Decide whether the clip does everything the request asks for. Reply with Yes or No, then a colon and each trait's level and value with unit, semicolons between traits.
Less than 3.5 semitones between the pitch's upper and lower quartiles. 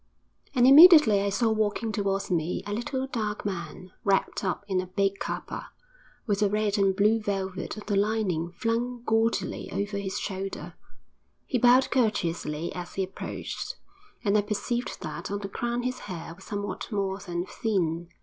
Yes: average, 2.8 semitones